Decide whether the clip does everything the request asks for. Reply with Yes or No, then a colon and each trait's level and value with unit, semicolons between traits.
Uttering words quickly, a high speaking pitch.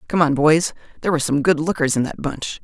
No: fast, 225 wpm; medium, 155 Hz